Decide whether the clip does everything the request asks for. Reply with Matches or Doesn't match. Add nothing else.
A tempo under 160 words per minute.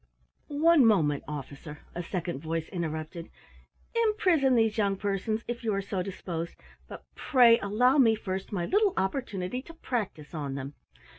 Matches